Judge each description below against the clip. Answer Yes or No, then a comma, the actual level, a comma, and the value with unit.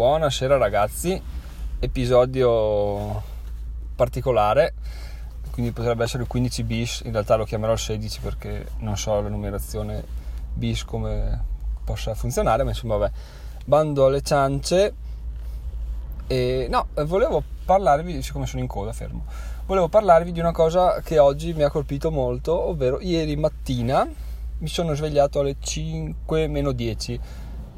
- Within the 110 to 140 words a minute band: Yes, average, 130 wpm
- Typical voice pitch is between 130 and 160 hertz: No, low, 115 Hz